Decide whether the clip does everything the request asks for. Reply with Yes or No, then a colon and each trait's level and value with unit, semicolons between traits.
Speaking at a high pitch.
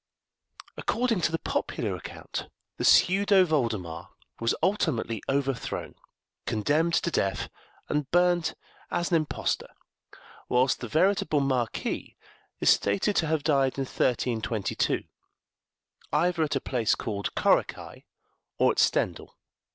No: medium, 140 Hz